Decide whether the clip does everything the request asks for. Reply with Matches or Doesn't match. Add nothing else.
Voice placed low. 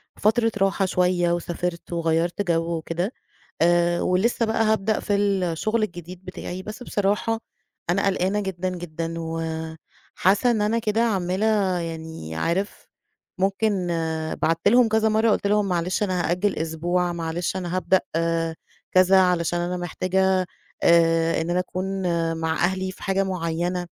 Doesn't match